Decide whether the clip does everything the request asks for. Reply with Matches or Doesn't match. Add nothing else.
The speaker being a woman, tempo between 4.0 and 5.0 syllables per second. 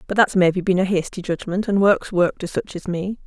Doesn't match